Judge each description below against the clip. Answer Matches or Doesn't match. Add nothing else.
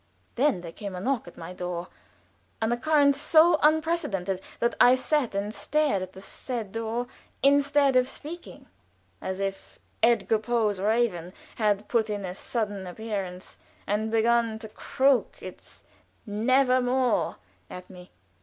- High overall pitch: Matches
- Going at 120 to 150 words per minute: Matches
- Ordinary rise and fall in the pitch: Matches